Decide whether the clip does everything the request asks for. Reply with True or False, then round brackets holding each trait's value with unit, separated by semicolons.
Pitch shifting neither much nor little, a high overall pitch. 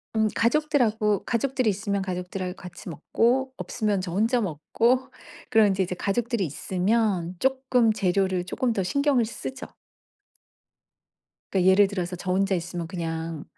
True (4.4 semitones; 200 Hz)